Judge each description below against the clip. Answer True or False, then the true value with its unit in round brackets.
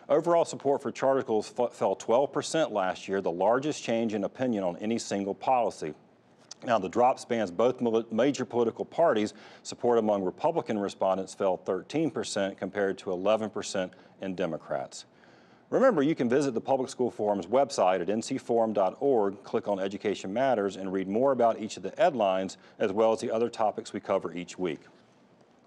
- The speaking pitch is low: True (110 Hz)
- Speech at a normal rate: True (170 wpm)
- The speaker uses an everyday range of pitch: True (3.4 semitones)